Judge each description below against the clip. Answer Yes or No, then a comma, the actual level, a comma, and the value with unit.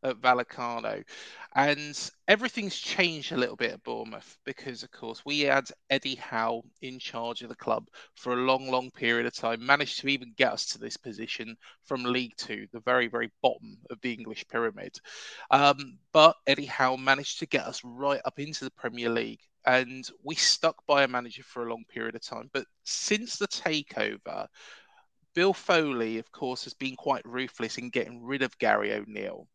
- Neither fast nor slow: Yes, average, 185 wpm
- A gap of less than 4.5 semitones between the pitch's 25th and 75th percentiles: Yes, average, 2.8 semitones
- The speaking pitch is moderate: No, low, 130 Hz